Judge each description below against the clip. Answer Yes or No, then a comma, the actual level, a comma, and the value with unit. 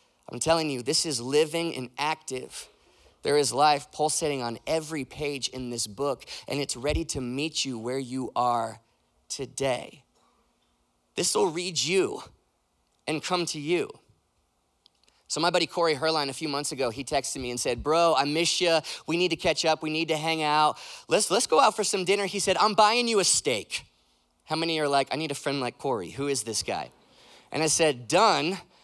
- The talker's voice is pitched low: No, medium, 150 Hz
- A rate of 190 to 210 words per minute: Yes, average, 200 wpm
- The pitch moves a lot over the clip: No, average, 3.9 semitones